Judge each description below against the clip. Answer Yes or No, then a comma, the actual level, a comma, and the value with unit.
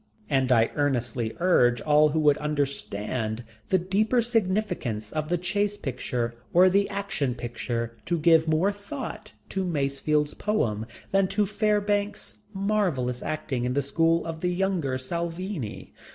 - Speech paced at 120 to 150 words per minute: Yes, average, 140 wpm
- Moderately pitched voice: Yes, medium, 160 Hz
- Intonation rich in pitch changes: Yes, wide, 7.3 semitones